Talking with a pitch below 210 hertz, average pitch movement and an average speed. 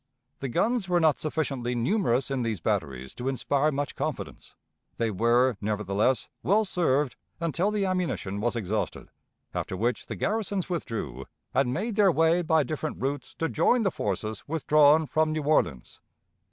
No: medium, 140 Hz; wide, 6.3 semitones; average, 155 wpm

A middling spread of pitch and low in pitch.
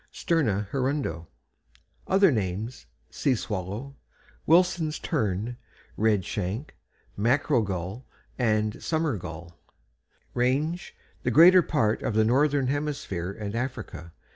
No: wide, 6.4 semitones; low, 120 Hz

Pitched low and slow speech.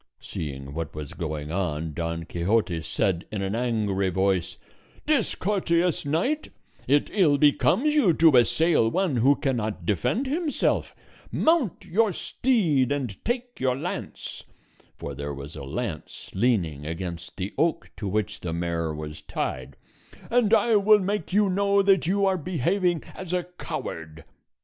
No: low, 125 Hz; average, 145 wpm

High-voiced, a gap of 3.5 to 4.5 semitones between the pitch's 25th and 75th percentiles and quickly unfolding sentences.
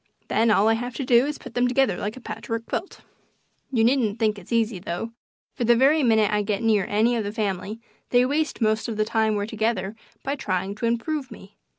No: high, 225 Hz; average, 2.7 semitones; fast, 235 wpm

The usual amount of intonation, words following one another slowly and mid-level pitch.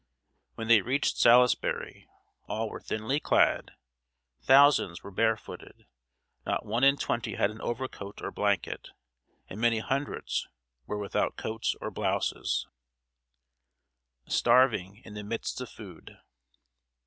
No: average, 3.3 semitones; slow, 125 wpm; low, 115 Hz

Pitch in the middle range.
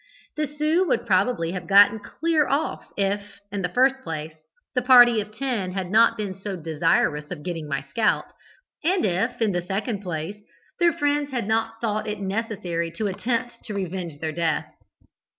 No: high, 205 Hz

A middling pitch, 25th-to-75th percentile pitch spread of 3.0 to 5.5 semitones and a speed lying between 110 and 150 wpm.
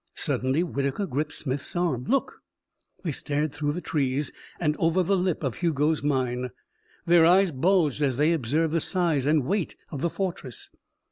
No: medium, 150 Hz; average, 3.9 semitones; average, 165 wpm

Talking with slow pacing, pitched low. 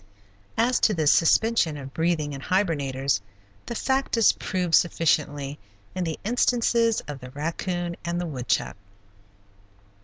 No: slow, 130 wpm; medium, 165 Hz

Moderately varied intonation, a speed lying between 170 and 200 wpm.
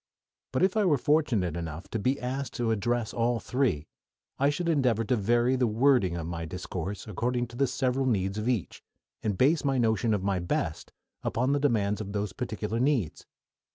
Yes: average, 4.6 semitones; average, 190 wpm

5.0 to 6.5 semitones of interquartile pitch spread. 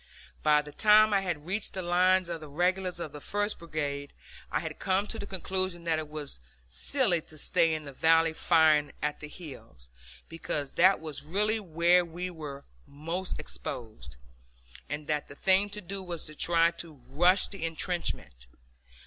No: average, 3.8 semitones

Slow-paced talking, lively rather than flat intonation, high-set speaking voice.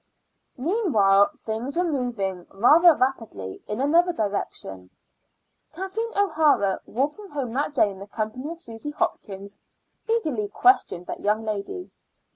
Yes: slow, 125 wpm; wide, 8.3 semitones; very high, 250 Hz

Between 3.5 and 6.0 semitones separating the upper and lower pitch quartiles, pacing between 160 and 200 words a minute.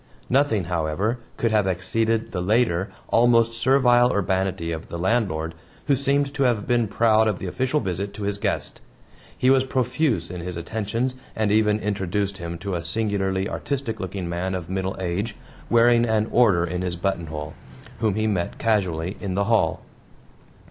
Yes: average, 4.2 semitones; average, 170 wpm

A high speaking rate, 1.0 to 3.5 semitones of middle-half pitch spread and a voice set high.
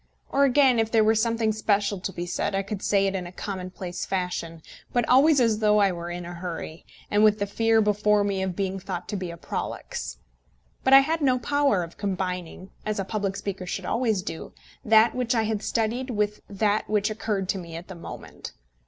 Yes: fast, 215 wpm; average, 3.2 semitones; high, 205 Hz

